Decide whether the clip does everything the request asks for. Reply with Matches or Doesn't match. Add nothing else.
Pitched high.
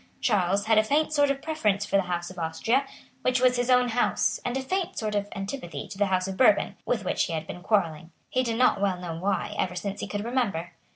Matches